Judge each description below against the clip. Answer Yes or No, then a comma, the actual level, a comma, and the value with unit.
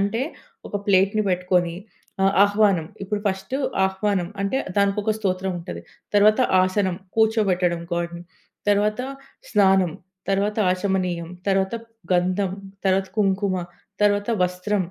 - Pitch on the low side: No, high, 195 Hz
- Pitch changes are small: Yes, narrow, 2.1 semitones